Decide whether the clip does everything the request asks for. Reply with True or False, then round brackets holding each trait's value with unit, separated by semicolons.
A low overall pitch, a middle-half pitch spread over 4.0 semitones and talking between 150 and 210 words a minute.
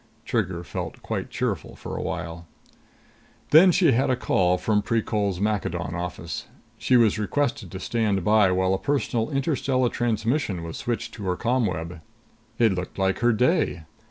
True (105 Hz; 4.9 semitones; 155 wpm)